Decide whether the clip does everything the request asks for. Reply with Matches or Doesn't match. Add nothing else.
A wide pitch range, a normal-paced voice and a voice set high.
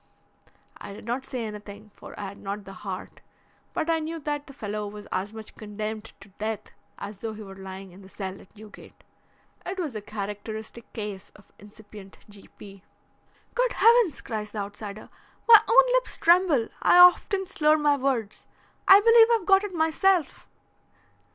Matches